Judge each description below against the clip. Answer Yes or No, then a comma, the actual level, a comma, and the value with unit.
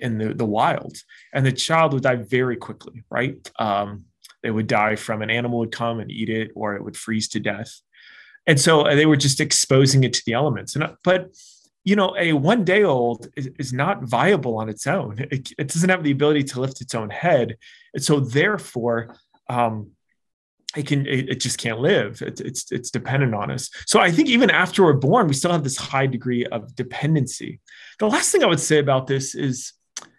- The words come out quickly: Yes, fast, 215 wpm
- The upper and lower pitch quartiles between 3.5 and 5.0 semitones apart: Yes, average, 4.6 semitones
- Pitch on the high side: No, low, 135 Hz